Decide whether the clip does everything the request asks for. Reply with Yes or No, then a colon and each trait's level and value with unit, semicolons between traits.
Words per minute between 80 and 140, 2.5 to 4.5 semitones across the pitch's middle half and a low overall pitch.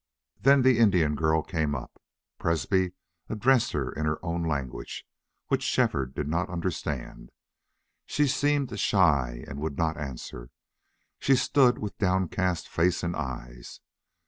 No: slow, 135 wpm; wide, 5.6 semitones; very low, 85 Hz